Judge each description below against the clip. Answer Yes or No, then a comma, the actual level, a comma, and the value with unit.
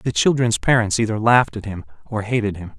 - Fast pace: Yes, fast, 215 wpm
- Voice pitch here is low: Yes, low, 105 Hz